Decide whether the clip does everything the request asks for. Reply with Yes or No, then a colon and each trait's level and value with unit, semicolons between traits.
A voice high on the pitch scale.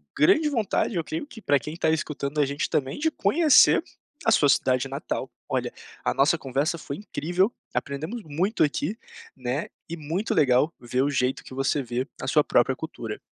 No: medium, 150 Hz